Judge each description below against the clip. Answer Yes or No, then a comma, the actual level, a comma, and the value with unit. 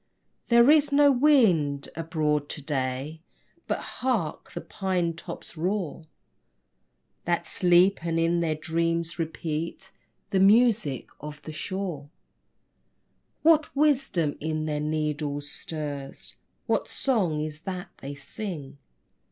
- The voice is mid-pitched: Yes, medium, 165 Hz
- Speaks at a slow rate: Yes, slow, 115 wpm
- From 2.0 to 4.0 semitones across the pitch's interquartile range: No, average, 4.4 semitones